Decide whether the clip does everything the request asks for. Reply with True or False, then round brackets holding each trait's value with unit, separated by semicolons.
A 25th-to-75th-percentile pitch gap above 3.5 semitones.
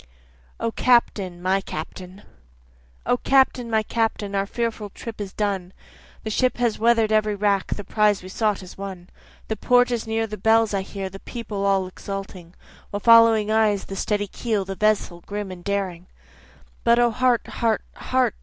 False (2.7 semitones)